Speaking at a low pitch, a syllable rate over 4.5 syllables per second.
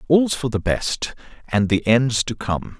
No: low, 120 Hz; 4.0 syllables/s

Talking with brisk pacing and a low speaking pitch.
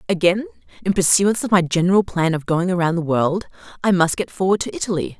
No: fast, 210 wpm; high, 190 Hz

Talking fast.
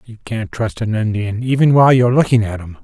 Yes: fast, 255 wpm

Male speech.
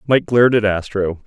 Yes: male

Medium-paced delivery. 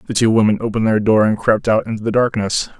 No: fast, 255 wpm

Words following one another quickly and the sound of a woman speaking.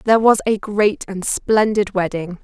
No: average, 175 wpm; female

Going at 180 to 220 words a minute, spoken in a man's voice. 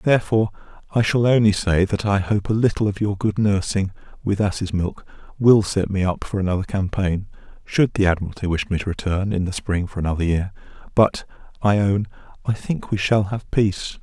Yes: average, 195 wpm; male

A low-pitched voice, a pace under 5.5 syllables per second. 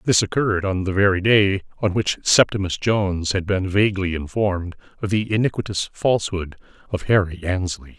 No: very low, 95 Hz; 5.6 syllables/s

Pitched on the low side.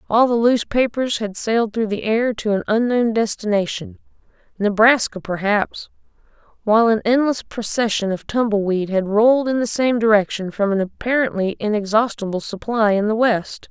No: high, 220 Hz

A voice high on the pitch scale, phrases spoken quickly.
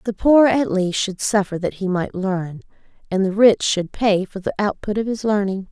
Yes: high, 200 Hz; fast, 220 wpm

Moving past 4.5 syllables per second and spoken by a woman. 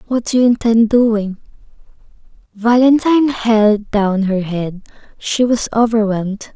No: 4.1 syllables/s; female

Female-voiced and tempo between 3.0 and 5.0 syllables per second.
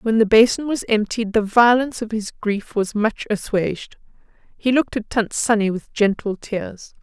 Yes: female; 4.8 syllables/s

